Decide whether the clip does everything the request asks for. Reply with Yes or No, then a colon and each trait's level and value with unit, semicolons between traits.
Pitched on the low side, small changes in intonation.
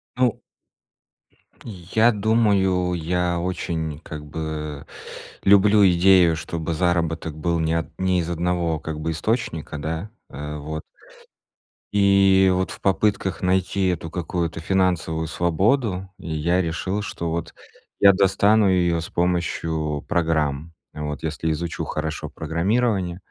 No: very low, 85 Hz; average, 3.0 semitones